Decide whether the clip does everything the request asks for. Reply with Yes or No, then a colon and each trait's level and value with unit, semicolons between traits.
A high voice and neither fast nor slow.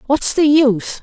Yes: very high, 270 Hz; average, 175 wpm